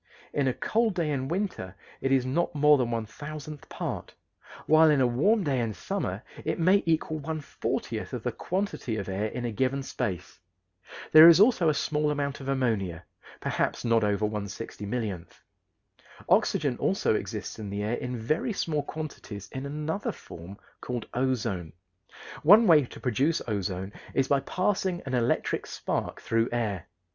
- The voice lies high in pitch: No, low, 130 Hz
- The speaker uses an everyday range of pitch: No, wide, 6.2 semitones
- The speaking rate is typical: Yes, average, 170 wpm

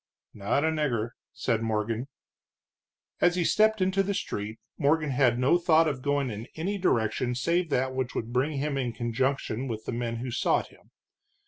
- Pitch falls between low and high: No, low, 130 Hz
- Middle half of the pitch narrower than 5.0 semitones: No, average, 5.3 semitones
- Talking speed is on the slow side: No, average, 180 wpm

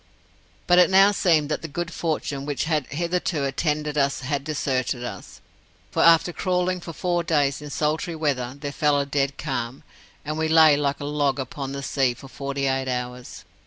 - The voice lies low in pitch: No, medium, 145 Hz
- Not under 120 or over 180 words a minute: No, average, 190 wpm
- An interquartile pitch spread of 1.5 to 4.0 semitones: Yes, average, 2.9 semitones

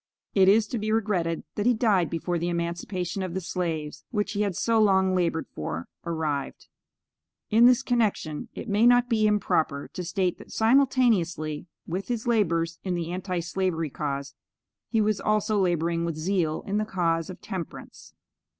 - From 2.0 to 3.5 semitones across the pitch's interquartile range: No, average, 4.2 semitones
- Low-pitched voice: No, medium, 185 Hz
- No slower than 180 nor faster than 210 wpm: No, average, 170 wpm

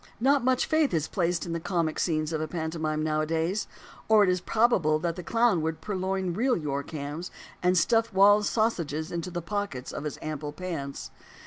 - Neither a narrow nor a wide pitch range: Yes, average, 4.6 semitones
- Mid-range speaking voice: Yes, medium, 170 Hz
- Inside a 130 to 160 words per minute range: No, average, 190 wpm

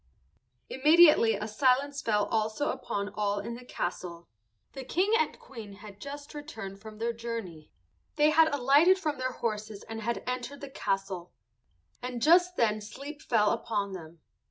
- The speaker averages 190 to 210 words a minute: No, average, 155 wpm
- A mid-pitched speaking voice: No, high, 230 Hz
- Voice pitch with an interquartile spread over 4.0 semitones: Yes, wide, 5.4 semitones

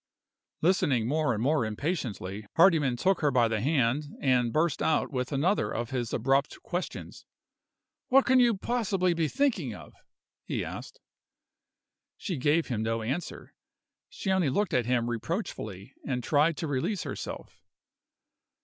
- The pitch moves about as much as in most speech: No, wide, 6.4 semitones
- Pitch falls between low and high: Yes, medium, 145 Hz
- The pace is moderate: Yes, average, 145 wpm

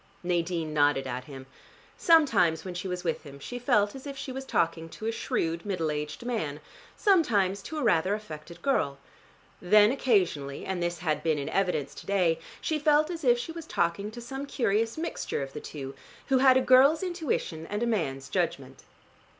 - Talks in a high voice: Yes, high, 195 Hz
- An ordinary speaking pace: Yes, average, 190 wpm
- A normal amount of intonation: No, wide, 8.2 semitones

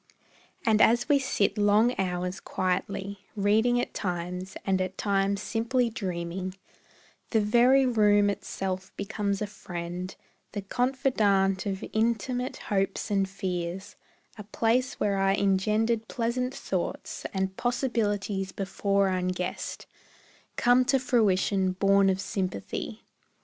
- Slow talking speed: Yes, slow, 120 wpm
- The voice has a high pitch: Yes, high, 200 Hz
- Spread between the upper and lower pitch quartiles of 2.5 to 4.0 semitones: Yes, average, 3.1 semitones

